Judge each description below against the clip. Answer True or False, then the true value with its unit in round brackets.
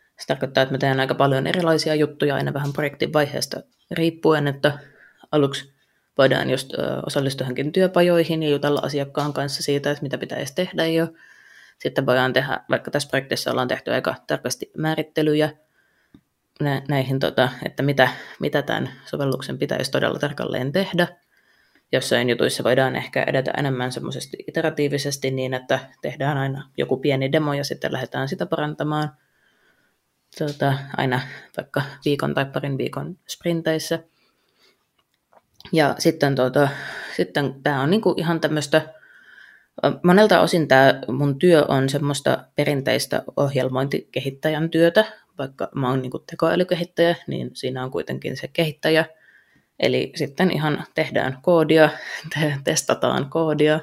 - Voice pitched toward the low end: False (145 Hz)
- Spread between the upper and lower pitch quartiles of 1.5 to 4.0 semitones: True (2.9 semitones)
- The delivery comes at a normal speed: True (130 wpm)